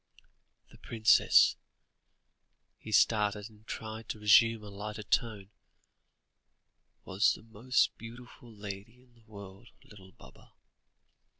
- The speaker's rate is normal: No, slow, 110 wpm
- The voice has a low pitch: Yes, low, 110 Hz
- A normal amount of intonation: No, narrow, 1.8 semitones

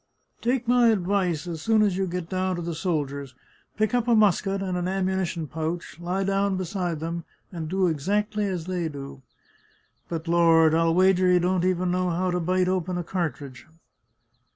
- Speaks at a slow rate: No, average, 180 wpm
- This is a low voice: No, medium, 180 Hz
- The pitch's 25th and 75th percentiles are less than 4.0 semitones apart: Yes, narrow, 2.5 semitones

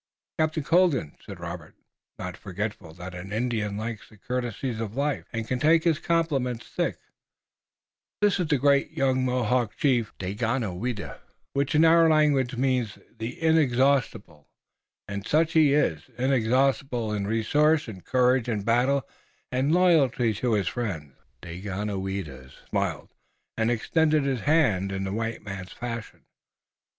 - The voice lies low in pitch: Yes, low, 120 Hz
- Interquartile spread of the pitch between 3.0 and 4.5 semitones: No, average, 5.2 semitones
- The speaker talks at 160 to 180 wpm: No, average, 140 wpm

